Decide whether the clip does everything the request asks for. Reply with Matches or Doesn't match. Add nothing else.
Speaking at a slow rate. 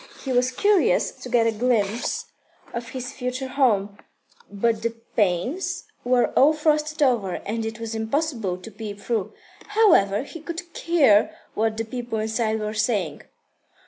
Doesn't match